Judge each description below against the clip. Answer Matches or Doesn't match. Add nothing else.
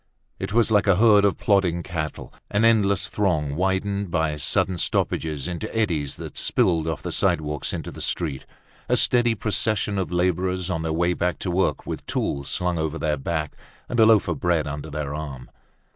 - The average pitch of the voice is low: Matches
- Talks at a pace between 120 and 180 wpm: Doesn't match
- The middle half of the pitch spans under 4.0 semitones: Doesn't match